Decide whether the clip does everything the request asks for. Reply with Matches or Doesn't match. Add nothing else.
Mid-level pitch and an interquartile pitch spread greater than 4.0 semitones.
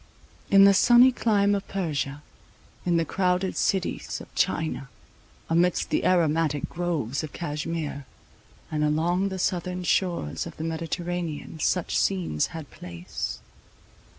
Doesn't match